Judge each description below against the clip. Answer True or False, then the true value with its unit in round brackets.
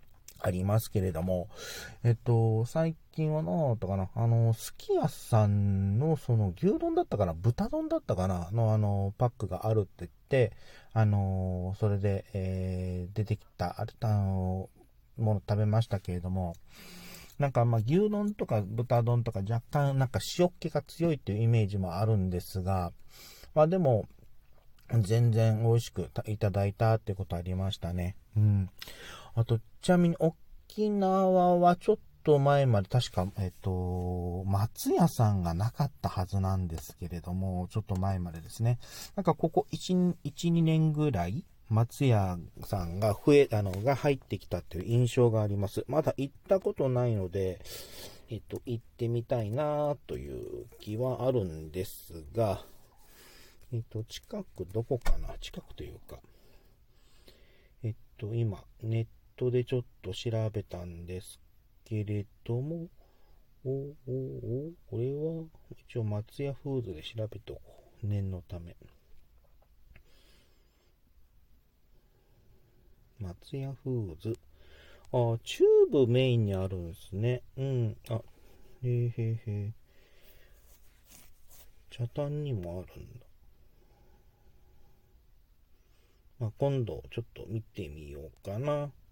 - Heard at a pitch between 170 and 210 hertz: False (110 Hz)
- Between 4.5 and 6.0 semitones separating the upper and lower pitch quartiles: True (5.4 semitones)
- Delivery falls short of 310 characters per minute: True (255 characters per minute)